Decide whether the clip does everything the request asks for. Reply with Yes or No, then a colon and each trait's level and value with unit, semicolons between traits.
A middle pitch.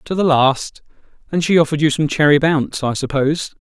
Yes: medium, 150 Hz